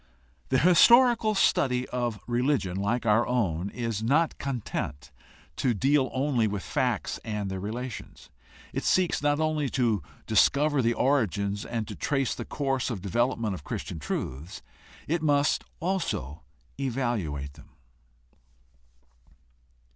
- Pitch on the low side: Yes, low, 120 Hz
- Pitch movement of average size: No, wide, 5.8 semitones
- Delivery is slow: Yes, slow, 130 wpm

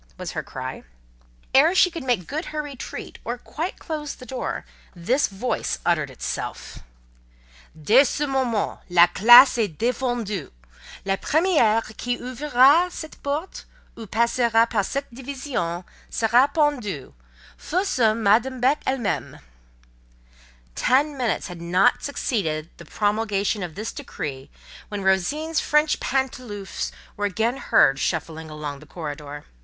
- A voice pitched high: Yes, high, 235 Hz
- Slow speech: Yes, slow, 130 wpm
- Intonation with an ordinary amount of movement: No, wide, 6.4 semitones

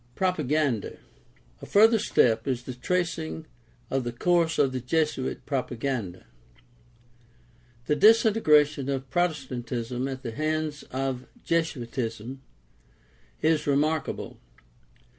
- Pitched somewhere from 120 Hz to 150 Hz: Yes, medium, 140 Hz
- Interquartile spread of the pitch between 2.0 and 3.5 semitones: No, average, 4.2 semitones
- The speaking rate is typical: No, slow, 105 wpm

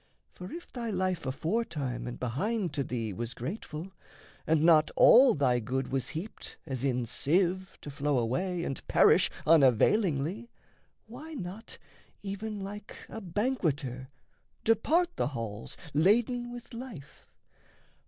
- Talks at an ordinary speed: No, slow, 130 wpm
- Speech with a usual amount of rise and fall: No, wide, 8.5 semitones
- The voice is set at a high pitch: No, medium, 170 Hz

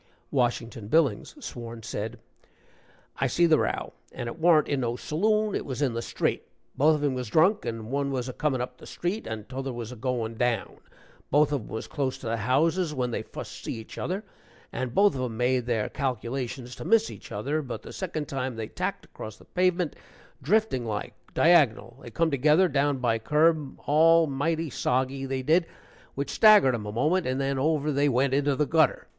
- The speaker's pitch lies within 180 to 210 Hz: No, low, 135 Hz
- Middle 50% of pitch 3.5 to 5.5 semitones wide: Yes, average, 4.5 semitones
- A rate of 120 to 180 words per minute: No, fast, 205 wpm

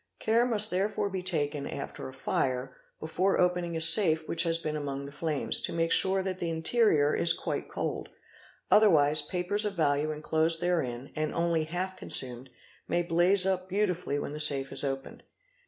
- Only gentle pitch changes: No, average, 4.1 semitones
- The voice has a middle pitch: Yes, medium, 165 Hz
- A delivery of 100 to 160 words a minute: No, average, 175 wpm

